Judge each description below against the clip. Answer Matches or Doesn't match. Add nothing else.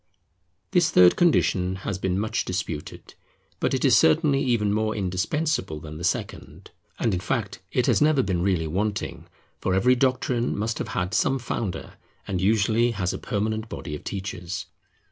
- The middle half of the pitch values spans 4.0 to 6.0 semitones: Matches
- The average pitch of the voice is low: Matches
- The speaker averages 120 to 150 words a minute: Doesn't match